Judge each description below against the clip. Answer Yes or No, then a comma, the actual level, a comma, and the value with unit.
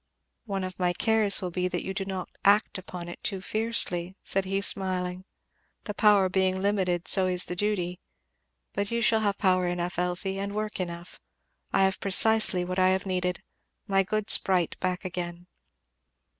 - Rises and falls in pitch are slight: Yes, narrow, 1.9 semitones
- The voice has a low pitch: No, high, 190 Hz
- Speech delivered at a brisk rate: No, average, 175 wpm